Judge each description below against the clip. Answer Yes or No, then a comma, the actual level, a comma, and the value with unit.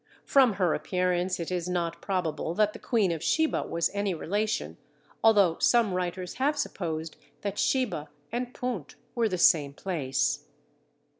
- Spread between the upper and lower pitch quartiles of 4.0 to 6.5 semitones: Yes, average, 4.5 semitones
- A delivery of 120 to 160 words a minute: Yes, average, 150 wpm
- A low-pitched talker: No, medium, 185 Hz